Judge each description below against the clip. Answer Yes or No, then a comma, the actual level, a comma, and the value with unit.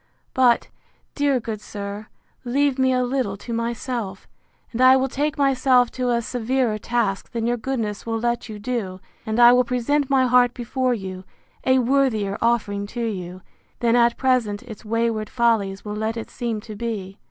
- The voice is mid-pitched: No, high, 235 Hz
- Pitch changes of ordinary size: Yes, average, 3.0 semitones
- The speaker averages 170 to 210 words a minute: Yes, average, 175 wpm